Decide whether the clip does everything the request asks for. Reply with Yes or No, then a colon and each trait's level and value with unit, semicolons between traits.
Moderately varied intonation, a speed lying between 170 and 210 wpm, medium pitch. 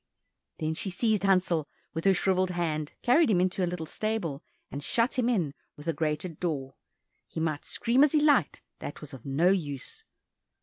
No: wide, 5.7 semitones; average, 185 wpm; medium, 175 Hz